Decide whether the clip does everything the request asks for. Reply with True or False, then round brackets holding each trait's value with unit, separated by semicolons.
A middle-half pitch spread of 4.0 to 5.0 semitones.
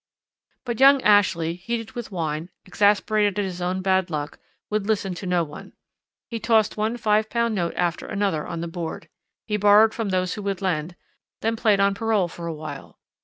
False (3.6 semitones)